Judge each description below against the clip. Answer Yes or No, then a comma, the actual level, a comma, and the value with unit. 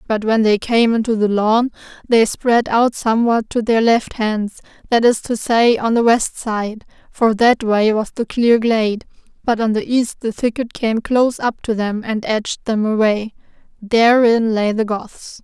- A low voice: No, high, 225 Hz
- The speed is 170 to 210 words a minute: Yes, average, 190 wpm